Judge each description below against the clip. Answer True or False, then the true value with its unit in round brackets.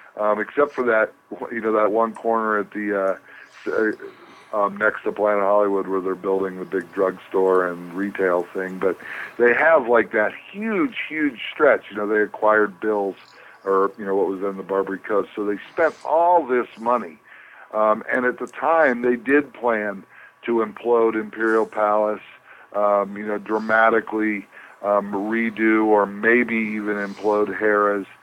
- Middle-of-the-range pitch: False (105 Hz)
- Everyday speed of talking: True (165 wpm)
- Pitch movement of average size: False (2.1 semitones)